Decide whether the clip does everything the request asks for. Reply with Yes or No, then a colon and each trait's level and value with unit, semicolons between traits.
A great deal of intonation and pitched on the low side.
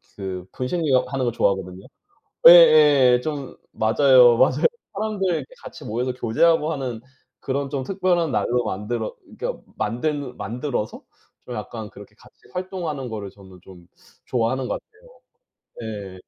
Yes: wide, 5.7 semitones; low, 130 Hz